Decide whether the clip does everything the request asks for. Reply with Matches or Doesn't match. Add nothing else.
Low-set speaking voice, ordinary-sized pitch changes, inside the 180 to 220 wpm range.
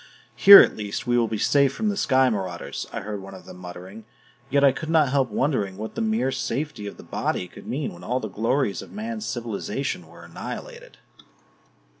Doesn't match